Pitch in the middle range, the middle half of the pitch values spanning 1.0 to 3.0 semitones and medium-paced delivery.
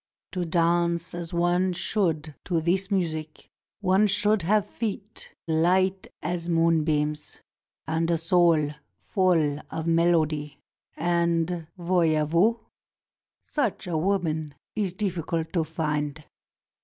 No: medium, 170 Hz; average, 2.7 semitones; slow, 110 wpm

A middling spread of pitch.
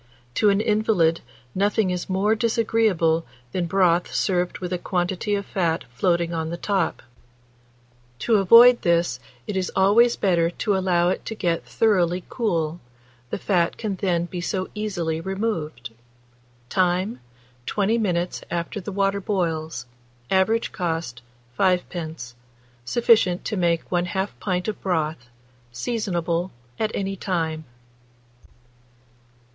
Yes: average, 3.2 semitones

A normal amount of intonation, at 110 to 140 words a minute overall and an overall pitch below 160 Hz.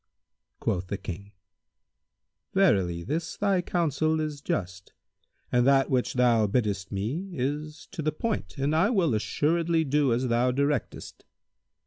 No: wide, 6.8 semitones; slow, 135 wpm; medium, 140 Hz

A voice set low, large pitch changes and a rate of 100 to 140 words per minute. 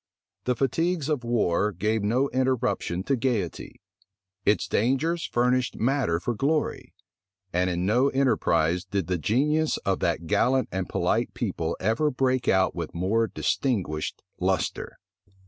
Yes: low, 115 Hz; wide, 6.2 semitones; slow, 135 wpm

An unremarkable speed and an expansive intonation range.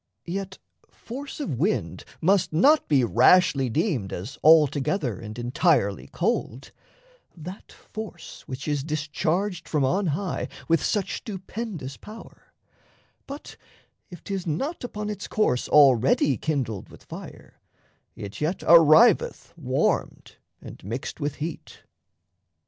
No: slow, 120 wpm; wide, 6.6 semitones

